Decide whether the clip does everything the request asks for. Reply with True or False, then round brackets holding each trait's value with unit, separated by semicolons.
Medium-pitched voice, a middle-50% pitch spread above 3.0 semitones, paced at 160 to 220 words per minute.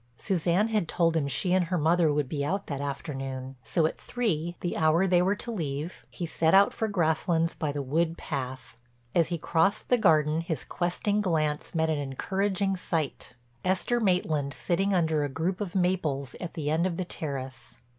True (165 Hz; 3.8 semitones; 180 wpm)